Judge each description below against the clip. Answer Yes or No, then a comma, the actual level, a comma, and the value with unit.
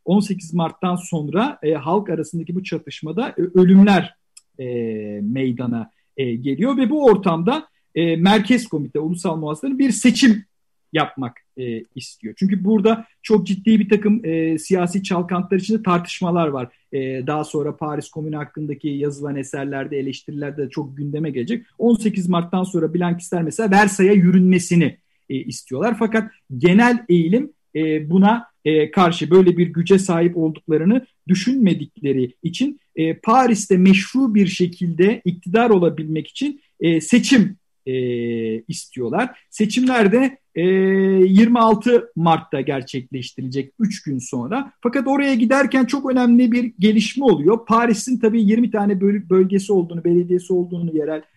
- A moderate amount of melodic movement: No, wide, 6.0 semitones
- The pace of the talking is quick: No, average, 125 wpm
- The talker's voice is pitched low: No, medium, 180 Hz